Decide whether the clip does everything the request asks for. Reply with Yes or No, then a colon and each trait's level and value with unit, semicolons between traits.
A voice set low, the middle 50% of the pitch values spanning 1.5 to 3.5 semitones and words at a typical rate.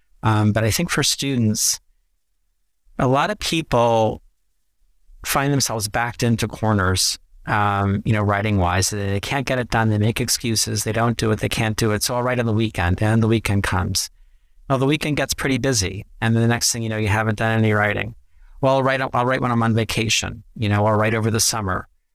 No: low, 110 Hz; average, 2.9 semitones; fast, 215 wpm